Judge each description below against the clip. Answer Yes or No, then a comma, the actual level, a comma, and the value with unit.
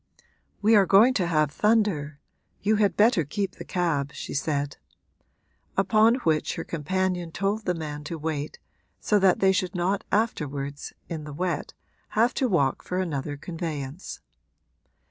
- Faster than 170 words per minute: No, average, 150 wpm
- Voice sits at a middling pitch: Yes, medium, 175 Hz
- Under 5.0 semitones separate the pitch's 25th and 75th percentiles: No, average, 5.3 semitones